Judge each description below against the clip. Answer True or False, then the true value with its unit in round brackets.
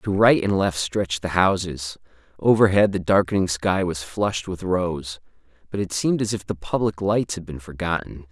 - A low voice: True (95 Hz)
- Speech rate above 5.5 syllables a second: False (5.1 syllables/s)